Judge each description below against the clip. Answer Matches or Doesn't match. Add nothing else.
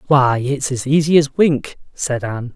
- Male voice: Matches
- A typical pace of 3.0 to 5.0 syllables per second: Matches